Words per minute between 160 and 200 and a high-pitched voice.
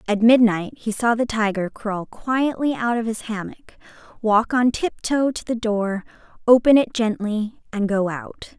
Yes: average, 175 wpm; high, 220 Hz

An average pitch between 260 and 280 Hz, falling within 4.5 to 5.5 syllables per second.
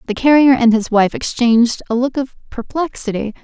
No: high, 245 Hz; 5.4 syllables/s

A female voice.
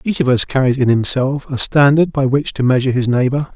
No: male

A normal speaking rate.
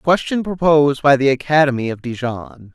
Yes: average, 155 wpm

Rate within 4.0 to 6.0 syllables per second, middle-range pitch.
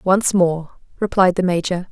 Yes: 4.6 syllables/s; medium, 180 Hz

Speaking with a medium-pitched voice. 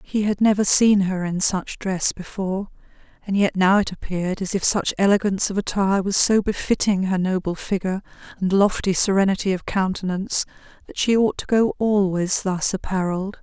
No: high, 195 Hz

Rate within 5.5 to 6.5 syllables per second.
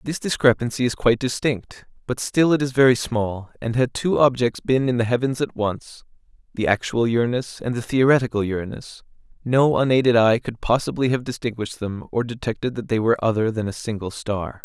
Yes: 5.6 syllables/s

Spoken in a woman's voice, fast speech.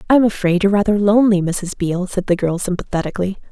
No: female; average, 190 wpm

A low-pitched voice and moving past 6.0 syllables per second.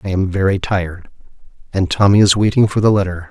Yes: very low, 95 Hz; 6.2 syllables/s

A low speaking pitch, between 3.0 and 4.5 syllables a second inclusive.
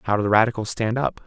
No: low, 110 Hz; 7.2 syllables/s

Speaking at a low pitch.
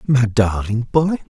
Yes: low, 120 Hz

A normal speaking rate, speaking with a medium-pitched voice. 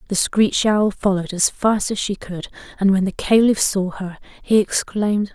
No: average, 190 wpm; high, 200 Hz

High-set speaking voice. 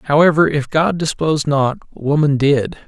No: medium, 150 Hz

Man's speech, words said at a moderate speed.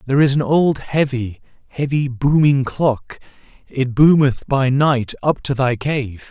Yes: male; average, 150 wpm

